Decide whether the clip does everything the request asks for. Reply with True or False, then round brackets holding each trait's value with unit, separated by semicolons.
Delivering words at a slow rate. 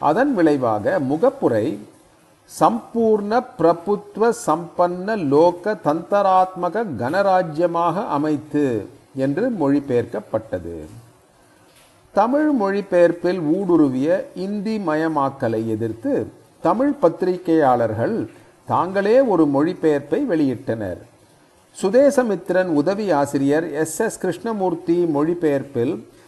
True (65 wpm)